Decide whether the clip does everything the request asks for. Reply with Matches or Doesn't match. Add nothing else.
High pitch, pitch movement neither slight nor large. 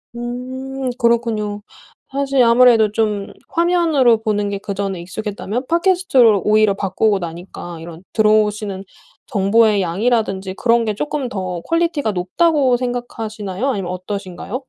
Matches